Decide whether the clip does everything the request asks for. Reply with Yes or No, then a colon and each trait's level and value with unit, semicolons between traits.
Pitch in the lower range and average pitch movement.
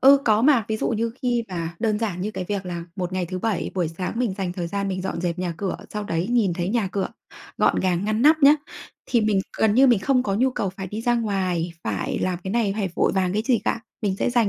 No: high, 200 Hz; average, 3.9 semitones